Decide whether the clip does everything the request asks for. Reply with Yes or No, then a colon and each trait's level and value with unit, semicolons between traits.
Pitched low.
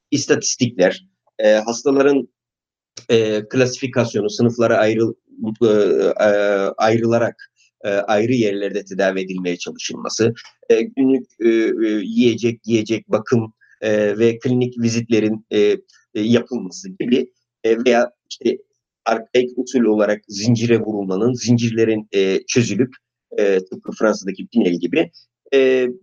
Yes: low, 115 Hz